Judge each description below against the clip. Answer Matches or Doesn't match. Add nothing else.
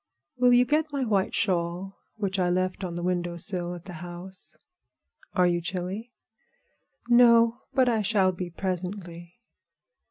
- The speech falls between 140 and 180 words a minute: Matches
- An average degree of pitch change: Matches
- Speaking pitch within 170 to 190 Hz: Matches